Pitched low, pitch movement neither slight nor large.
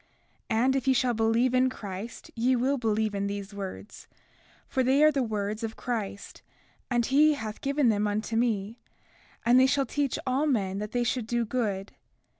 No: high, 235 Hz; average, 3.6 semitones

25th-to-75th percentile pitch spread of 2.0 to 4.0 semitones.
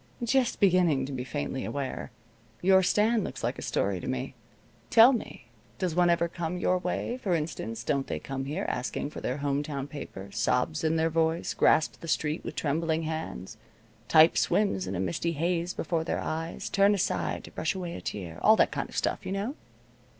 No: average, 4.8 semitones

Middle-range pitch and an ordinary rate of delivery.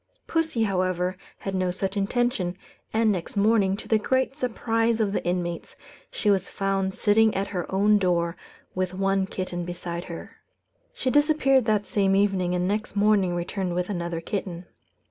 No: high, 195 Hz; average, 165 wpm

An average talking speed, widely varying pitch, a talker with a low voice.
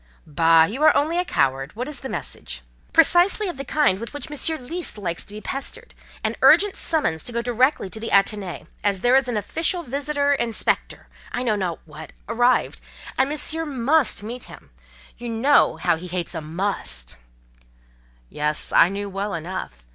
No: average, 170 wpm; wide, 8.0 semitones; high, 230 Hz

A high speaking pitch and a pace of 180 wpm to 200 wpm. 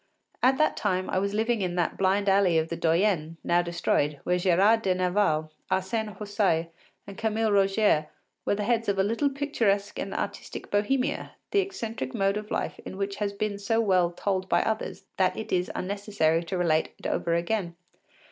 Yes: high, 195 Hz; average, 185 wpm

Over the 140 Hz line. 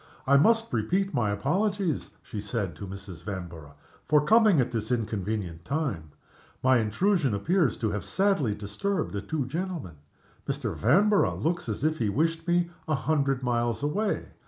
No: low, 130 Hz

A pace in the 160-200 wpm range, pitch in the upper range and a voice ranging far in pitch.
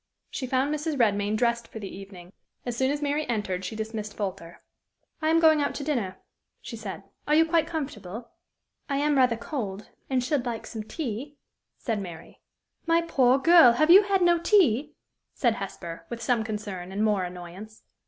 Yes: average, 185 wpm; high, 235 Hz; wide, 6.2 semitones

